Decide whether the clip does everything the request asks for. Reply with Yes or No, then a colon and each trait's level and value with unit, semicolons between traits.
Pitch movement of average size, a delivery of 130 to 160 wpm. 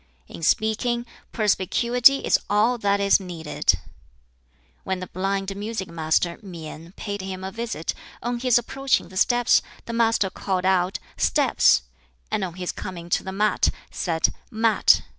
Yes: average, 3.9 semitones; average, 145 wpm